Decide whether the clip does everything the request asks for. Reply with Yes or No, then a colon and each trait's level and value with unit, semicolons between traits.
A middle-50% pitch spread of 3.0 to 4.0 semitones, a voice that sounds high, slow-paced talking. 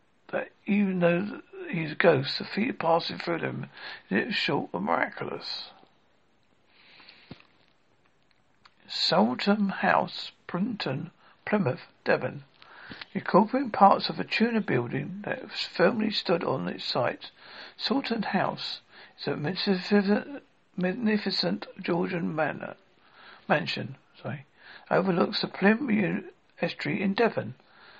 Yes: average, 3.6 semitones; high, 200 Hz; slow, 110 wpm